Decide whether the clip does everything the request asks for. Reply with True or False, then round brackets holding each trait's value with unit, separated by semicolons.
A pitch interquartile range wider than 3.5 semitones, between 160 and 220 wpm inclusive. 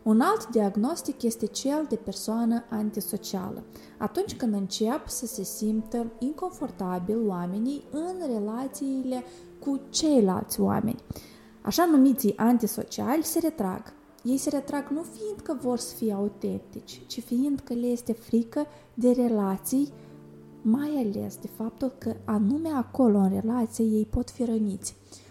False (4.5 semitones; 135 wpm)